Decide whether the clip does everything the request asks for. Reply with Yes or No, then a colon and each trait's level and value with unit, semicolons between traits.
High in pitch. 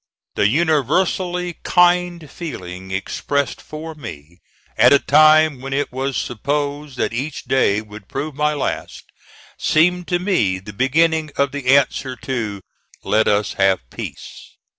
No: medium, 140 Hz